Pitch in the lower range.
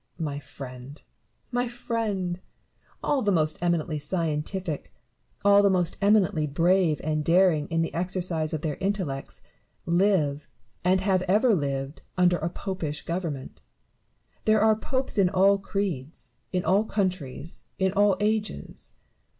No: medium, 180 Hz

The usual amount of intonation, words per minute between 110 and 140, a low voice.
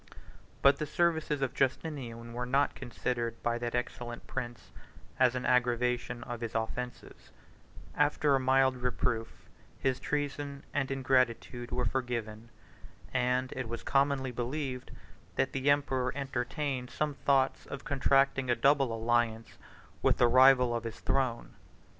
No: narrow, 2.3 semitones; slow, 135 wpm; low, 125 Hz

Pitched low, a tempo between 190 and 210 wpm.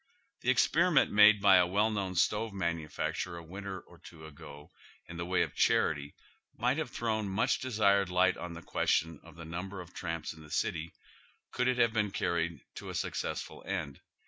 Yes: very low, 90 Hz; average, 195 wpm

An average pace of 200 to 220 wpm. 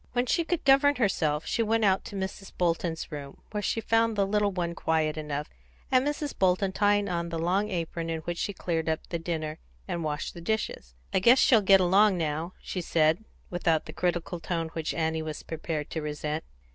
Yes: fast, 205 wpm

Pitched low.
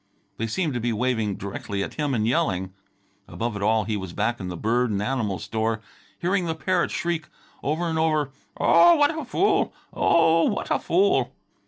Yes: low, 125 Hz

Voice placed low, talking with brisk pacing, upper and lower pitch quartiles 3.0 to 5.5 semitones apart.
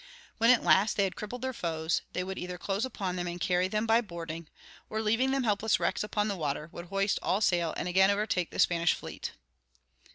No: high, 190 Hz; fast, 220 wpm; average, 3.5 semitones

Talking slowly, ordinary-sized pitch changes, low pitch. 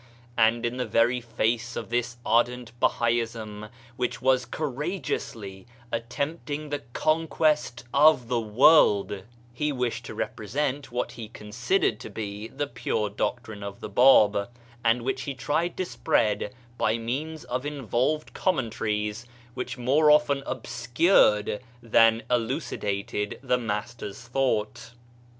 Yes: slow, 130 wpm; average, 3.5 semitones; low, 120 Hz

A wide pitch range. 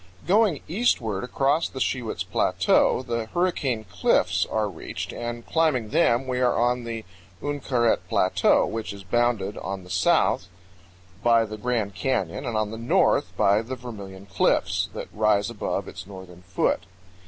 No: average, 3.8 semitones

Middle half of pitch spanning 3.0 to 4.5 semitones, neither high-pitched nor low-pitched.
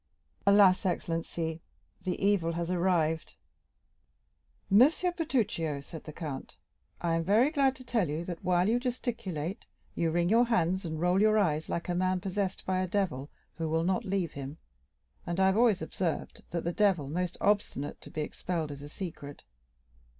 Yes: average, 3.8 semitones; medium, 180 Hz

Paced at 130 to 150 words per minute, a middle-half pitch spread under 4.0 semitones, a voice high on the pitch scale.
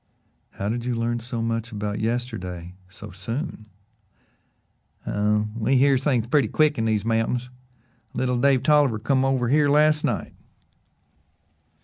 No: slow, 135 wpm; average, 3.6 semitones; low, 120 Hz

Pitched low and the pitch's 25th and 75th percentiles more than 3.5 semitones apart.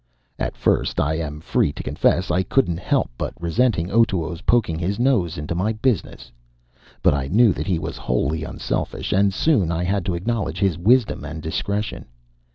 Yes: very low, 90 Hz; average, 4.8 semitones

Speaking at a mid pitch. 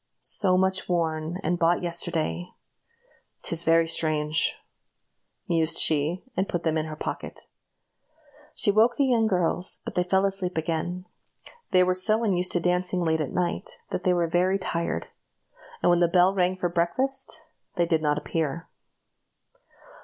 Yes: medium, 175 Hz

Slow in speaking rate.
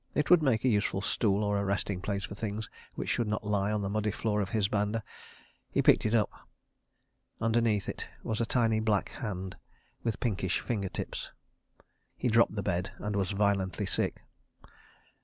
No: average, 180 wpm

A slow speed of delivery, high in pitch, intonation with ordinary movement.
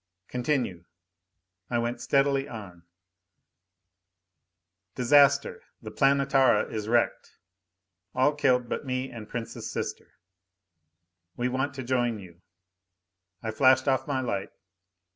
No: slow, 105 wpm; low, 125 Hz; average, 3.0 semitones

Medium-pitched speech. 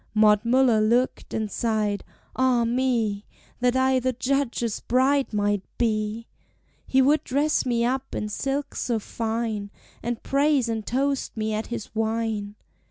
No: high, 235 Hz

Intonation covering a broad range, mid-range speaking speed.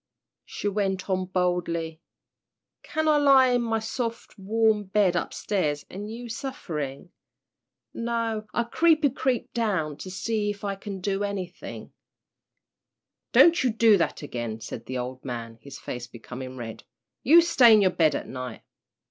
Yes: wide, 7.2 semitones; average, 155 wpm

